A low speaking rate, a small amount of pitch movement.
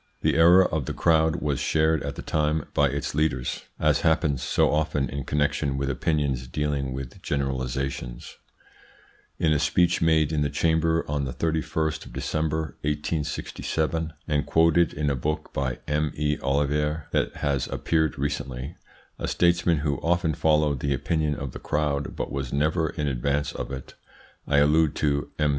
No: average, 165 wpm; narrow, 2.2 semitones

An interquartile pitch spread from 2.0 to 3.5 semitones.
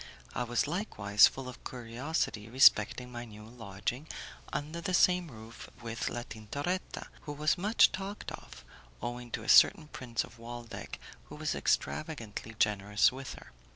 No: average, 5.3 semitones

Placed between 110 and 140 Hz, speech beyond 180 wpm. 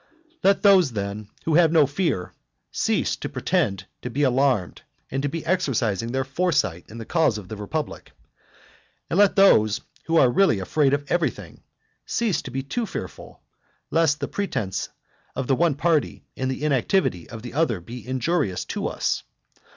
No: low, 135 Hz; average, 175 wpm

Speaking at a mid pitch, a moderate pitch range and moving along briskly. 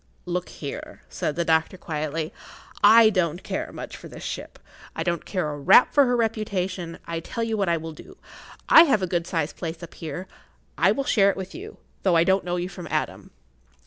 Yes: medium, 180 Hz; average, 3.8 semitones; fast, 215 wpm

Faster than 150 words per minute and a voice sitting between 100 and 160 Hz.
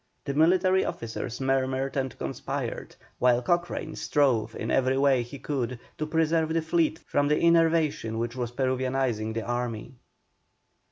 No: average, 145 wpm; low, 135 Hz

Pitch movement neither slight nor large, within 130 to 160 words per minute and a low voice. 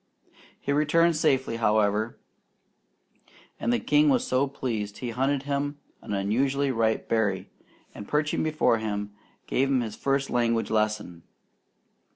Yes: average, 4.8 semitones; slow, 135 wpm; low, 125 Hz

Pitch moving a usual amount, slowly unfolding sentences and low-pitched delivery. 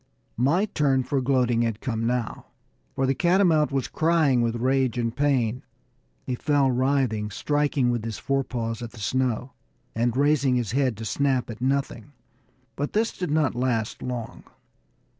No: average, 3.2 semitones; average, 160 wpm; low, 130 Hz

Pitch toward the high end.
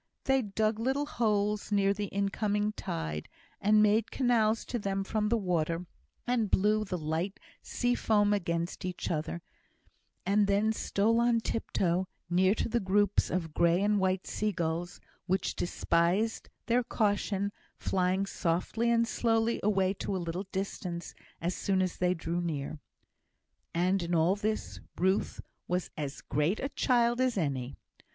Yes: high, 195 Hz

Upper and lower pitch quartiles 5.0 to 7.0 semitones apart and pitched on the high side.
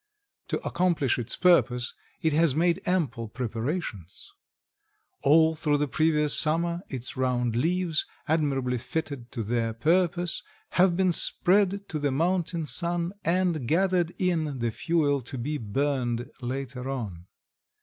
No: wide, 5.4 semitones; medium, 150 Hz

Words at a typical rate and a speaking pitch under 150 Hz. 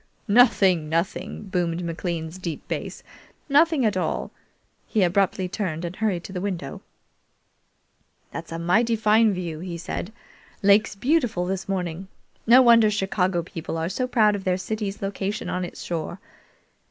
No: average, 155 wpm; high, 190 Hz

